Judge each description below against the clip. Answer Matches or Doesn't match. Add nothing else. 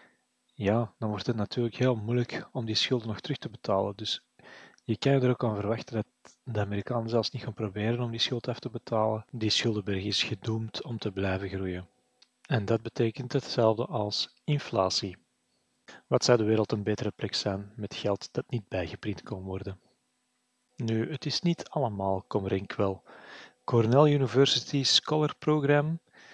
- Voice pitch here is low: Matches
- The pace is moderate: Matches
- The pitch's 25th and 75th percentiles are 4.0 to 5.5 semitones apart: Doesn't match